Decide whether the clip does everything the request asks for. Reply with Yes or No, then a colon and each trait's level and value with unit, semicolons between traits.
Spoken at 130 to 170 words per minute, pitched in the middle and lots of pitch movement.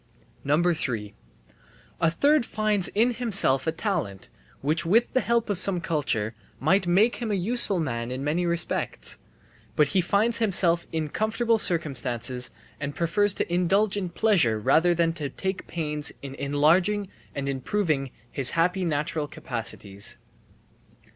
Yes: average, 140 wpm; medium, 170 Hz; wide, 6.1 semitones